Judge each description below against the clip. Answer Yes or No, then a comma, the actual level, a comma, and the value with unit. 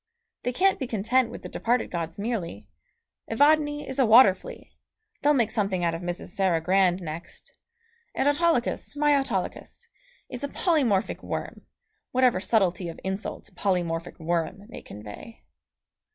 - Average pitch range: No, wide, 7.0 semitones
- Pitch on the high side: Yes, high, 210 Hz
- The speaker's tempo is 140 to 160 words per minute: Yes, average, 145 wpm